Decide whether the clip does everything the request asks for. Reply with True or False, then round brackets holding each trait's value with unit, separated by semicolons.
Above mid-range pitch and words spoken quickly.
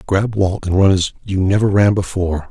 False (95 Hz; 215 wpm)